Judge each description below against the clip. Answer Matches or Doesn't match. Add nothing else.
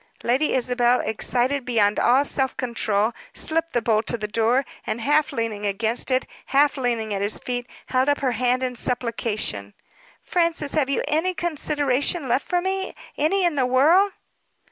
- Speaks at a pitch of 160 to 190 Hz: Doesn't match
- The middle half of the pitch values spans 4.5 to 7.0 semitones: Doesn't match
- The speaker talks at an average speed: Matches